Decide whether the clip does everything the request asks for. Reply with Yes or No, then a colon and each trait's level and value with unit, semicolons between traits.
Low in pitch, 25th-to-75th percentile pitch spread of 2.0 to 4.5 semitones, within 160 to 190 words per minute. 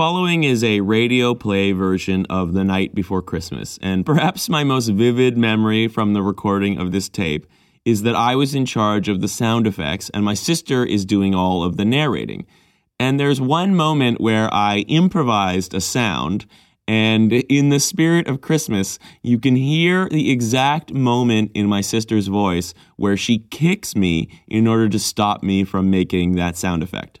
No: low, 110 Hz; average, 5.1 semitones; average, 180 wpm